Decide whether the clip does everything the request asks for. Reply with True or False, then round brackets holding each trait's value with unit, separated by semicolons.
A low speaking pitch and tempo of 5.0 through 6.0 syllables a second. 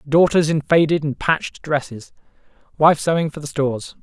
False (150 Hz; 5.2 syllables/s)